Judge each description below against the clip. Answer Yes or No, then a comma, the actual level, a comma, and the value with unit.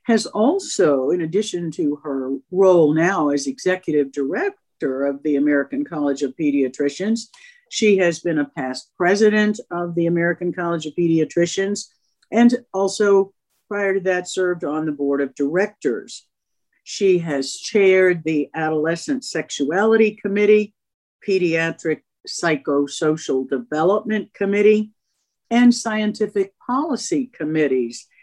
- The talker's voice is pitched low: No, medium, 180 Hz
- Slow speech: Yes, slow, 115 wpm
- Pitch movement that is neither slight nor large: No, wide, 5.8 semitones